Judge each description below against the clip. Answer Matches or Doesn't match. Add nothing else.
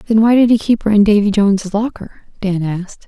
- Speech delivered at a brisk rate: Matches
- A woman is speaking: Matches